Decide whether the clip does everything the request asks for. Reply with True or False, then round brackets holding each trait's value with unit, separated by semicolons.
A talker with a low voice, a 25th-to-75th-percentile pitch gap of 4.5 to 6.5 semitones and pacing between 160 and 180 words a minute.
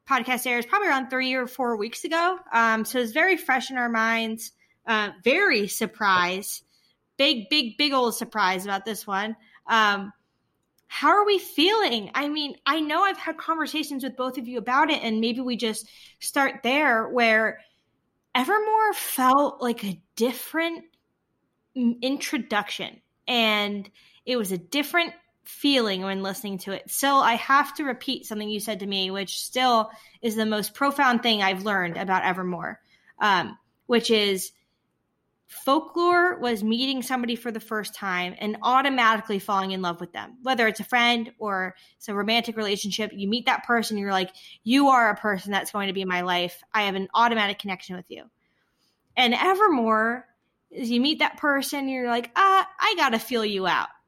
False (235 Hz; 4.8 semitones; 170 wpm)